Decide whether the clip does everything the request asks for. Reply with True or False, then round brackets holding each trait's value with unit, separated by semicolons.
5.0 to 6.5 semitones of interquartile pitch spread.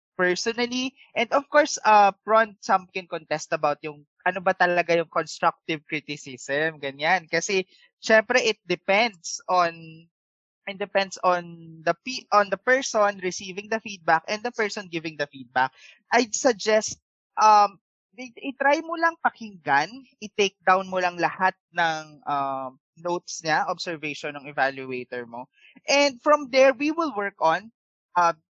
True (5.5 semitones)